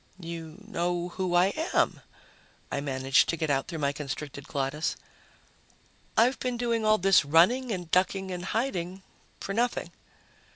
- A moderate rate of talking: Yes, average, 150 wpm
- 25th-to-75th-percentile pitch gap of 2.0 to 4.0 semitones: No, average, 4.5 semitones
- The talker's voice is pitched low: No, medium, 175 Hz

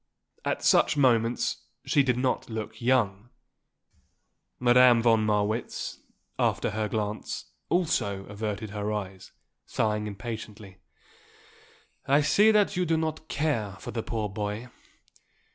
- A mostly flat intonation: No, average, 3.7 semitones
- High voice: No, low, 110 Hz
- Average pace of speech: No, slow, 120 wpm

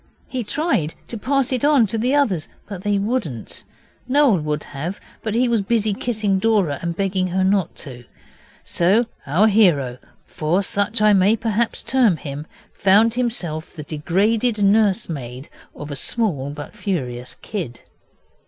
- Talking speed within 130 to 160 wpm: Yes, average, 155 wpm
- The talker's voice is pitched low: No, high, 200 Hz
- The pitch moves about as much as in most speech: No, wide, 6.3 semitones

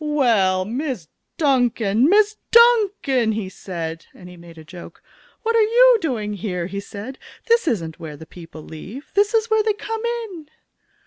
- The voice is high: Yes, high, 245 Hz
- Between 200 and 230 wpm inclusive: No, average, 170 wpm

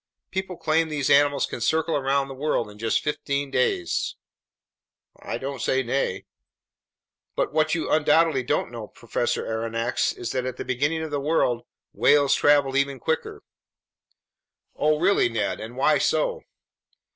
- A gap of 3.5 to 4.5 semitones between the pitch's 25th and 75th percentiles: Yes, average, 4.0 semitones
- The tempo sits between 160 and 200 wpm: No, average, 150 wpm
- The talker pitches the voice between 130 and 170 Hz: Yes, medium, 140 Hz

